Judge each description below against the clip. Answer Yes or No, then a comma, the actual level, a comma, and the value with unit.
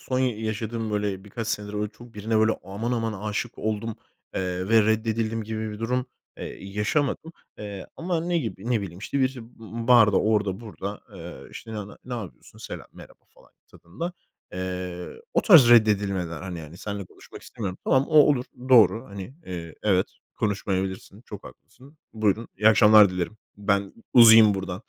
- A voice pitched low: Yes, low, 105 Hz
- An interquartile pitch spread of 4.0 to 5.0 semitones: No, average, 3.0 semitones